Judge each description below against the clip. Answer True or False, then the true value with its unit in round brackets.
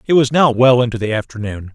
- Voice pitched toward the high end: False (120 Hz)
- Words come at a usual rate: False (240 wpm)